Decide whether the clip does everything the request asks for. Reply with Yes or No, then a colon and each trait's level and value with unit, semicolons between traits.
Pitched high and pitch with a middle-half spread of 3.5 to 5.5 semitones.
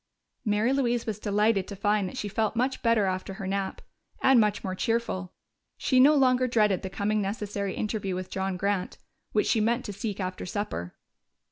No: high, 210 Hz; average, 3.0 semitones